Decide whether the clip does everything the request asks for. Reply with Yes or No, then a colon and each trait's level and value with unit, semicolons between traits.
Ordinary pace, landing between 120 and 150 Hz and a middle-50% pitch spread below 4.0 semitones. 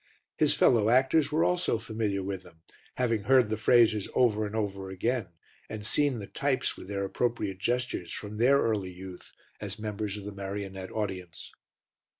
No: average, 165 wpm; low, 105 Hz; average, 3.6 semitones